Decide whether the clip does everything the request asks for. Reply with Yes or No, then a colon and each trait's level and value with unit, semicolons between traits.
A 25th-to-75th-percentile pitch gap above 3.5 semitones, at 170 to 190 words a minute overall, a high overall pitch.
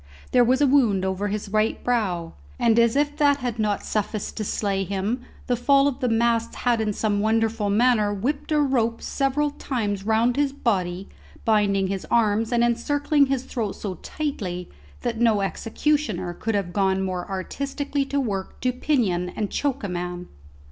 Yes: average, 4.6 semitones; average, 175 wpm; high, 225 Hz